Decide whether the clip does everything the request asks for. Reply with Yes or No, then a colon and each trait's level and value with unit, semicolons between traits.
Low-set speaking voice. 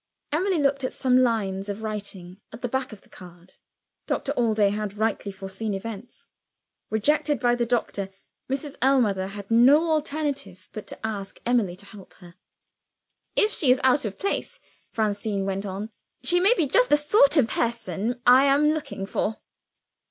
No: high, 230 Hz